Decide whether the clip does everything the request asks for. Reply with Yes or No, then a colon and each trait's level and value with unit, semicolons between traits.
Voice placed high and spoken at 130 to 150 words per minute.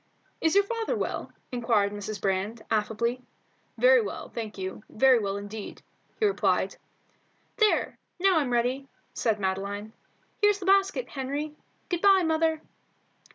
Yes: very high, 255 Hz; slow, 135 wpm